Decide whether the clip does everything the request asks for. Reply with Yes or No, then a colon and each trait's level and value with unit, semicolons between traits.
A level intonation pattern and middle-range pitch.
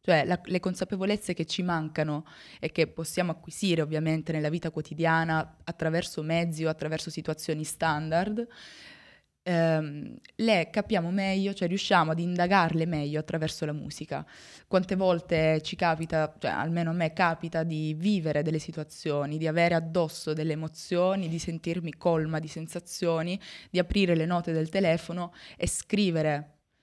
Yes: narrow, 2.1 semitones; medium, 165 Hz